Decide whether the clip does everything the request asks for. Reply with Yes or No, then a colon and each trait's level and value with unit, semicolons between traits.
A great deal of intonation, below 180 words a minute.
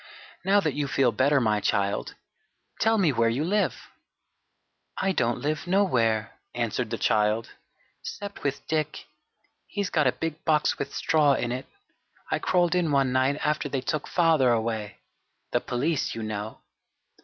Yes: wide, 5.8 semitones; average, 155 wpm